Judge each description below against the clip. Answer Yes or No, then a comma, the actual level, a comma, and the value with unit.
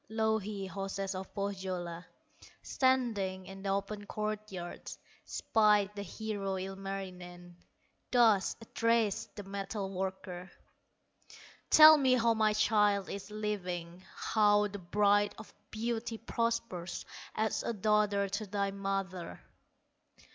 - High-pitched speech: Yes, high, 200 Hz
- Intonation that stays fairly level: Yes, narrow, 2.2 semitones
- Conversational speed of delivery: No, slow, 110 wpm